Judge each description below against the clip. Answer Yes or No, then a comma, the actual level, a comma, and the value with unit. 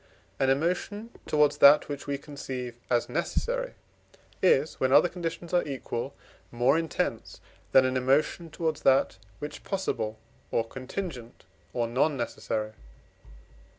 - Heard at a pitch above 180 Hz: No, medium, 140 Hz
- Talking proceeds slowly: Yes, slow, 125 wpm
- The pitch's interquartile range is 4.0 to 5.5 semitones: Yes, average, 4.6 semitones